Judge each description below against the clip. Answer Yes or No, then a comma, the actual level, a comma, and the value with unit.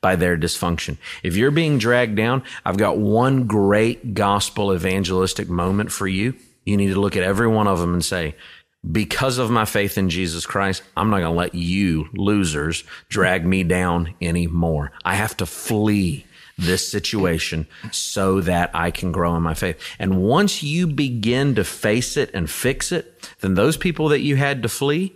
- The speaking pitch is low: Yes, low, 100 Hz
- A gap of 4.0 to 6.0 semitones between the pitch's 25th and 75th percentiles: Yes, average, 5.0 semitones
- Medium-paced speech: Yes, average, 185 wpm